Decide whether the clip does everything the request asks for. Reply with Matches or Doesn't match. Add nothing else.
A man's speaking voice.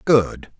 Matches